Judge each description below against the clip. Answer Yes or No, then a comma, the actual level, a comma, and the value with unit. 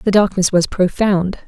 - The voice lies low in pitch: No, high, 190 Hz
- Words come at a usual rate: Yes, average, 165 wpm